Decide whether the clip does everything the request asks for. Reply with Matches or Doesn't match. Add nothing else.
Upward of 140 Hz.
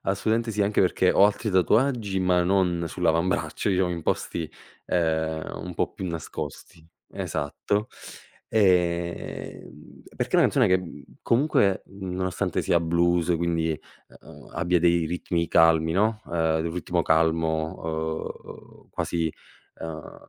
Doesn't match